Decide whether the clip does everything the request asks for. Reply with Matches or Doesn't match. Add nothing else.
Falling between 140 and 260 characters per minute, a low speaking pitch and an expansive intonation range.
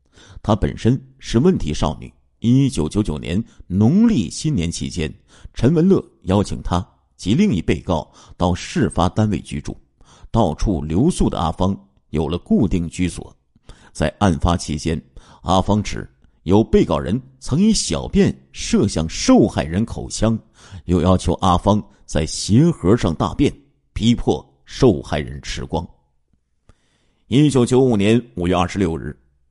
Matches